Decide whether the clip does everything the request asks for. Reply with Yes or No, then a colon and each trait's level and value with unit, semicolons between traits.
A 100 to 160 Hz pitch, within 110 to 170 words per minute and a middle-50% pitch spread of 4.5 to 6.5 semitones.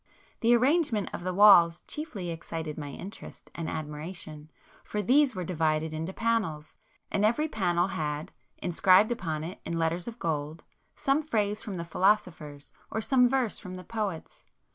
No: medium, 185 Hz; average, 160 wpm; wide, 5.4 semitones